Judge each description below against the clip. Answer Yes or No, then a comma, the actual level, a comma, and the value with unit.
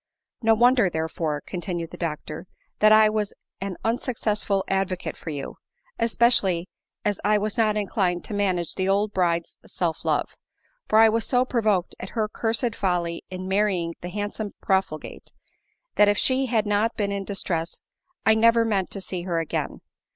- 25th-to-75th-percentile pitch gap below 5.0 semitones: Yes, average, 3.5 semitones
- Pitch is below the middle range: No, high, 200 Hz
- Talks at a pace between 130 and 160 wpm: No, average, 175 wpm